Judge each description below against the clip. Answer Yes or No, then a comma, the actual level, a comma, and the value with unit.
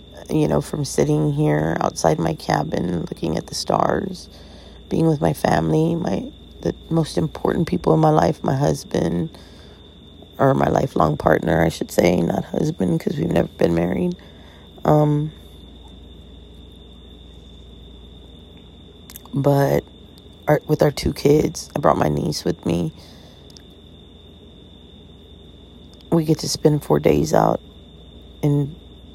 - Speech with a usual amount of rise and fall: No, narrow, 2.1 semitones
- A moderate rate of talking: No, slow, 125 wpm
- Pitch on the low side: Yes, very low, 80 Hz